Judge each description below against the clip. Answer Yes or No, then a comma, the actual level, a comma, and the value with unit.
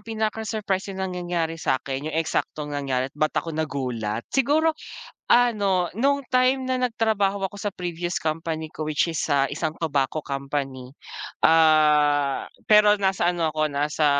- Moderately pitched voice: Yes, medium, 165 Hz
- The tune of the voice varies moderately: No, wide, 5.7 semitones